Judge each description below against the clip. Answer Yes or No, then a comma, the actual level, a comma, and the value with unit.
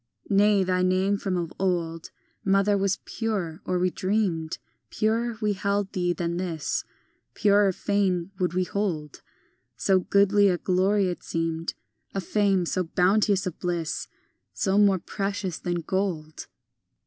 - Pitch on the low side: No, high, 190 Hz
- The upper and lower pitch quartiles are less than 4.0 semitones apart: Yes, narrow, 2.4 semitones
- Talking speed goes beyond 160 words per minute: No, average, 145 wpm